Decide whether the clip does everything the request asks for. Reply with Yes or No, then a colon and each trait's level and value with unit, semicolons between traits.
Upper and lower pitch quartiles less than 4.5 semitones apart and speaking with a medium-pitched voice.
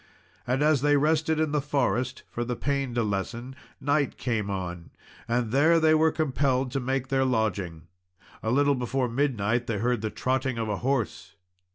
No: average, 3.6 semitones; low, 130 Hz